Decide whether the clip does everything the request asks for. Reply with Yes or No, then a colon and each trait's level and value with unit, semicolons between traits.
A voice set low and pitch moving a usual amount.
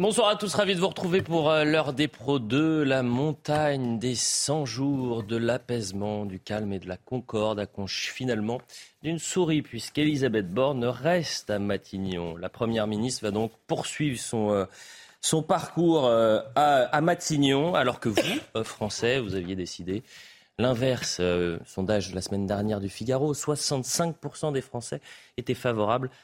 No: low, 125 Hz; wide, 6.1 semitones